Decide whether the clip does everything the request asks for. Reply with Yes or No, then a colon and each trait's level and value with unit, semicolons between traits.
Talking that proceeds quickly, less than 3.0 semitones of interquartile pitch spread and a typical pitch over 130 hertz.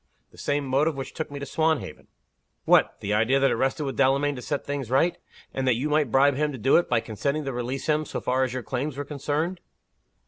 Yes: fast, 240 wpm; narrow, 2.4 semitones; medium, 140 Hz